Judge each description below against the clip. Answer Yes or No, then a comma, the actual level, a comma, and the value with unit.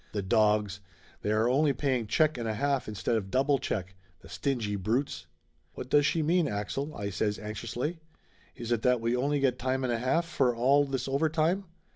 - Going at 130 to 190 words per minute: No, average, 200 wpm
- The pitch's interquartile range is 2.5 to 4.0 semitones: No, average, 4.7 semitones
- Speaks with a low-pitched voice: Yes, low, 125 Hz